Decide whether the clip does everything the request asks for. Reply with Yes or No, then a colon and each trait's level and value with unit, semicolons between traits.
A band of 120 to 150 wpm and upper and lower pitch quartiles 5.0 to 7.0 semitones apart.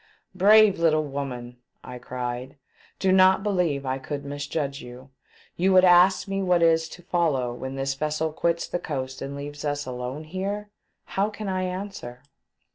No: average, 165 wpm; wide, 5.6 semitones